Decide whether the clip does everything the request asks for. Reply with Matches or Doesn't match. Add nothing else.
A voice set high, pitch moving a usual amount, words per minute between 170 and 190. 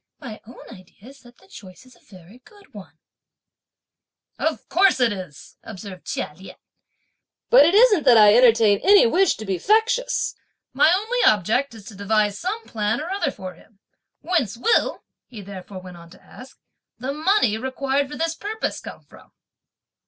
Doesn't match